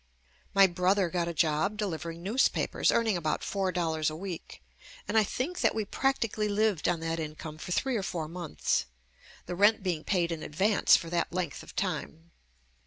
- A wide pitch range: No, average, 3.9 semitones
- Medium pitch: Yes, medium, 180 Hz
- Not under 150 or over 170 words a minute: No, average, 185 wpm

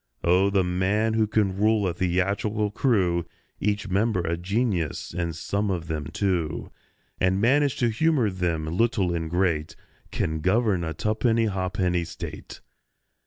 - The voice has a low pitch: Yes, very low, 95 Hz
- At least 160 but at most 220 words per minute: No, average, 145 wpm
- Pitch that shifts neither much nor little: Yes, average, 3.8 semitones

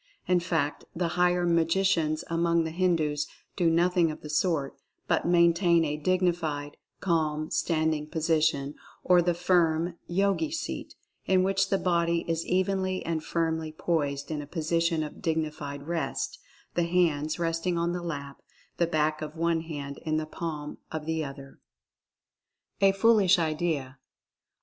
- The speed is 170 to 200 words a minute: No, average, 145 wpm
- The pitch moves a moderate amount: No, narrow, 2.3 semitones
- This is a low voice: No, medium, 165 Hz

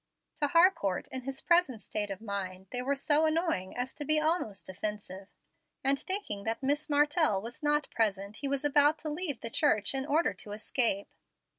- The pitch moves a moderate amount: No, wide, 6.4 semitones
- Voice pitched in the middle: No, very high, 270 Hz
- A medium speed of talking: Yes, average, 185 wpm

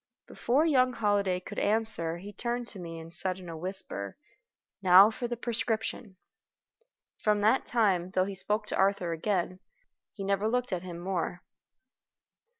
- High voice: Yes, high, 195 Hz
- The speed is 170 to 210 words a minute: No, average, 155 wpm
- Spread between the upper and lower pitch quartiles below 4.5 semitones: Yes, average, 3.6 semitones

